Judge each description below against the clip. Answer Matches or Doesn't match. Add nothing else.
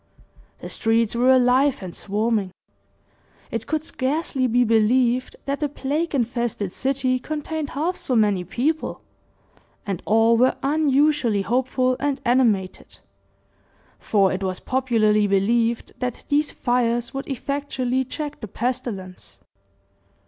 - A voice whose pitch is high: Matches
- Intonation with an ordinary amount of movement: Matches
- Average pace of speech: Doesn't match